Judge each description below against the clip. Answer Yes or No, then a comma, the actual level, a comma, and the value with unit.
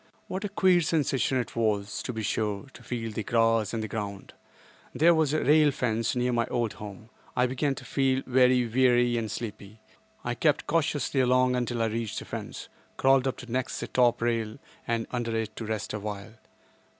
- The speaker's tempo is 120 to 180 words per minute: No, average, 195 wpm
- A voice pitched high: No, low, 120 Hz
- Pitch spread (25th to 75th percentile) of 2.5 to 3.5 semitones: Yes, average, 2.9 semitones